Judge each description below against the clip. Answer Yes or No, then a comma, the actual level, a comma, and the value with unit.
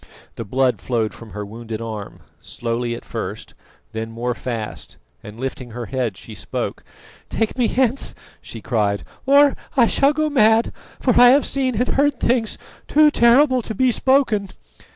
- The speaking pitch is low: No, high, 200 Hz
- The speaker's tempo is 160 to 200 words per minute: Yes, average, 165 wpm